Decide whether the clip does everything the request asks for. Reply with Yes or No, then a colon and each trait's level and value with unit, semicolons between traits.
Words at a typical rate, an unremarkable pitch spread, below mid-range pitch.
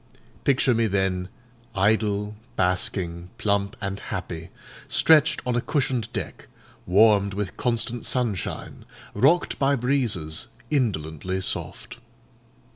No: slow, 105 wpm; average, 4.8 semitones; low, 105 Hz